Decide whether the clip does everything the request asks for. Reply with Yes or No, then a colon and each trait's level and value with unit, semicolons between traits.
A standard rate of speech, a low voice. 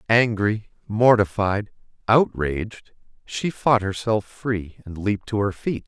No: slow, 125 wpm; low, 105 Hz